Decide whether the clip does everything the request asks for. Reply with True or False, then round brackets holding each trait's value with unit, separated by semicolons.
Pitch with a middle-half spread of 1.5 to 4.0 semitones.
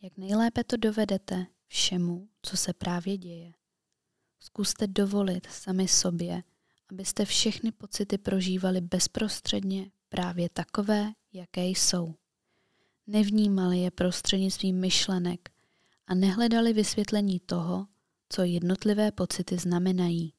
True (2.5 semitones)